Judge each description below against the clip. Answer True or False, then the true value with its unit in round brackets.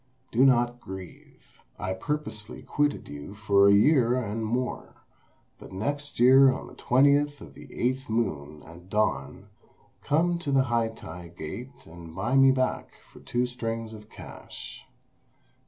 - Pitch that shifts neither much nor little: True (4.9 semitones)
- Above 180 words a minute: False (150 wpm)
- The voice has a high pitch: False (120 Hz)